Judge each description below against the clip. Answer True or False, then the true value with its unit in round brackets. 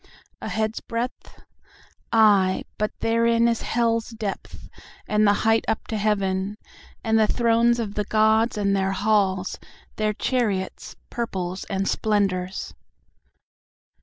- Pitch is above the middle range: True (215 Hz)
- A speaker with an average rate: False (120 wpm)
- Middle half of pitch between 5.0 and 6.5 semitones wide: False (2.6 semitones)